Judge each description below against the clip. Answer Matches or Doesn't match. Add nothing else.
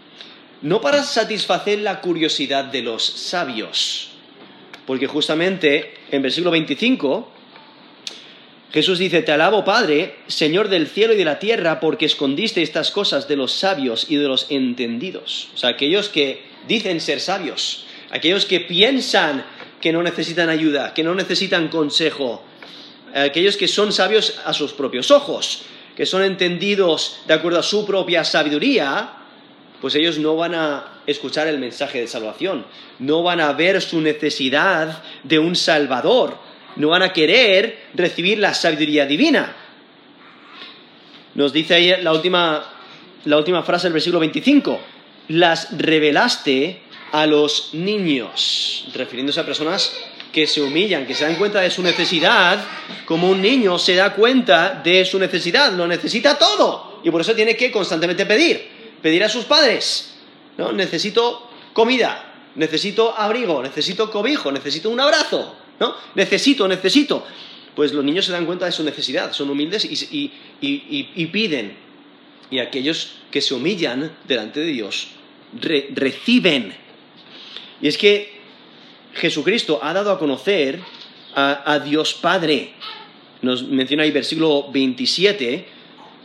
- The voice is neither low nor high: Matches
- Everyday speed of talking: Matches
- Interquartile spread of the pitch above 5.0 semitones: Matches